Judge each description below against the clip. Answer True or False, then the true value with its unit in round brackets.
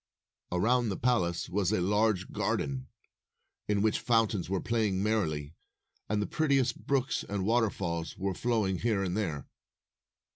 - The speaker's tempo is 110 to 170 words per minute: True (140 wpm)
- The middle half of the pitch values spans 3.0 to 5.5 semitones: True (3.9 semitones)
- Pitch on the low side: True (105 Hz)